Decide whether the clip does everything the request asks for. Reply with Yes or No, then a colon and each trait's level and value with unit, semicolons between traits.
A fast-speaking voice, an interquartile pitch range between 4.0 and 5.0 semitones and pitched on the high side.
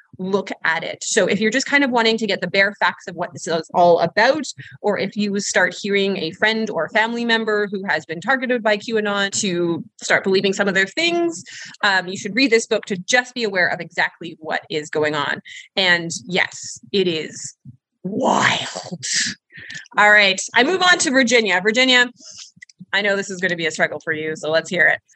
Yes: fast, 210 wpm; average, 4.3 semitones; high, 200 Hz